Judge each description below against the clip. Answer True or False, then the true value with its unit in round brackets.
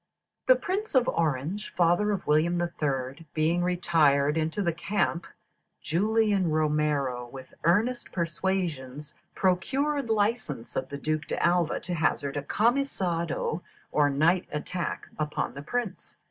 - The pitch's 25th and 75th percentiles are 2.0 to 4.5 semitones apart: False (4.9 semitones)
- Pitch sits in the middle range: True (170 Hz)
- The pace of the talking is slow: True (125 wpm)